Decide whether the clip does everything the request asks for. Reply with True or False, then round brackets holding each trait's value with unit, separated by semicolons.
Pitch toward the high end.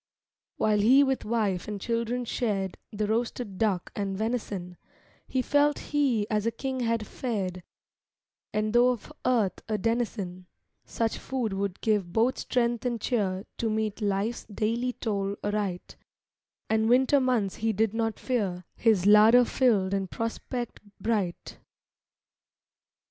True (220 Hz)